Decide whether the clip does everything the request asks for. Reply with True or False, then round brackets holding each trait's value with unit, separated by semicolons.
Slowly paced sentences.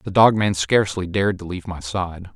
False (230 wpm)